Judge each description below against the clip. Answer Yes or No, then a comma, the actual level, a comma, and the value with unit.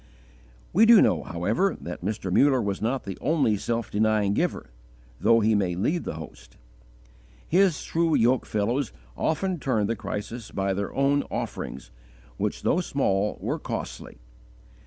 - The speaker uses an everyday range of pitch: No, wide, 6.0 semitones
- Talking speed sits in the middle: Yes, average, 150 wpm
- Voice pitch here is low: Yes, low, 115 Hz